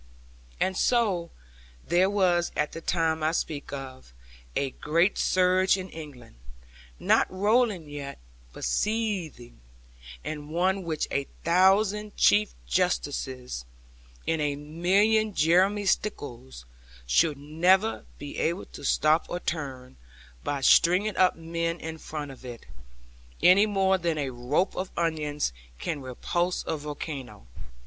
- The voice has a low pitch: No, medium, 165 Hz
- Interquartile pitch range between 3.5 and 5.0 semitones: Yes, average, 4.7 semitones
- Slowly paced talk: Yes, slow, 125 wpm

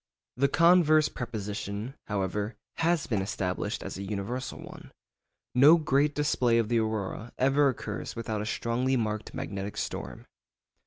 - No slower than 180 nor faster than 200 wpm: No, average, 140 wpm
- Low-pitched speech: Yes, low, 115 Hz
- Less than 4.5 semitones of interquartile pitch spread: No, average, 4.9 semitones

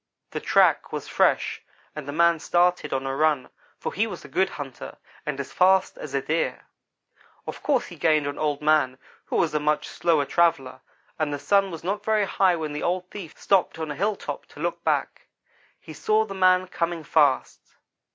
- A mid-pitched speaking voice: Yes, medium, 165 Hz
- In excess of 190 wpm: Yes, average, 200 wpm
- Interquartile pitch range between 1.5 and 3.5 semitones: No, average, 4.0 semitones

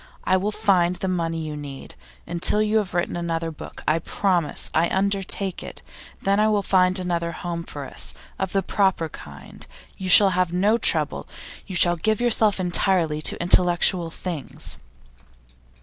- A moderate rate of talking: Yes, average, 165 wpm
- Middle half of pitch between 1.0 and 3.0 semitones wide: Yes, average, 2.7 semitones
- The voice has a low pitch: No, medium, 180 Hz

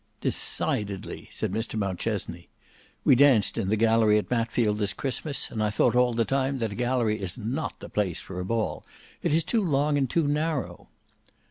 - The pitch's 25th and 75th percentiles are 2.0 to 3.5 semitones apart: No, average, 4.4 semitones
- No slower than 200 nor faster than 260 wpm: No, average, 190 wpm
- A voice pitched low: Yes, low, 115 Hz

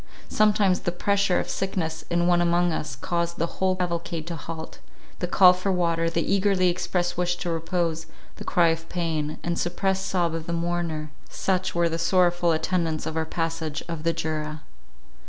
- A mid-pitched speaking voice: Yes, medium, 170 Hz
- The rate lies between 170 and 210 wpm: Yes, average, 175 wpm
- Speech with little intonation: Yes, narrow, 1.7 semitones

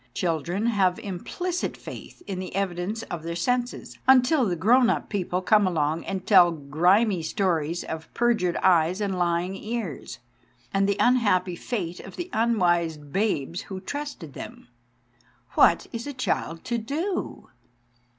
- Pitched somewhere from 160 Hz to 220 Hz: Yes, high, 190 Hz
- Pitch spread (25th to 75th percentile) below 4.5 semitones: No, average, 5.2 semitones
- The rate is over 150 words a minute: No, average, 145 wpm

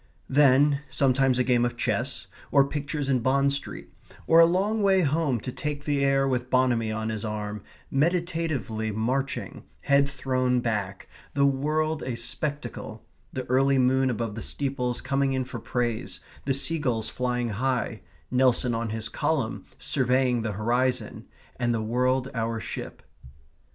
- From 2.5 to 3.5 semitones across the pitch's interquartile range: Yes, average, 3.0 semitones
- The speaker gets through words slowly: No, average, 155 wpm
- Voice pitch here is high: No, low, 130 Hz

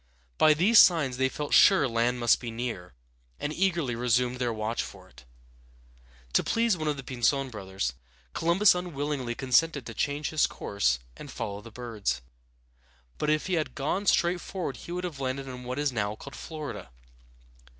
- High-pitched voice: No, low, 135 Hz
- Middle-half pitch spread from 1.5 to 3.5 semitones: No, average, 4.9 semitones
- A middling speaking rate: Yes, average, 180 wpm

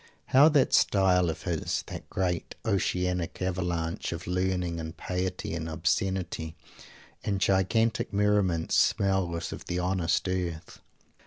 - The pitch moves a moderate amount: No, narrow, 2.2 semitones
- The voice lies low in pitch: Yes, very low, 90 Hz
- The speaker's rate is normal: No, slow, 125 wpm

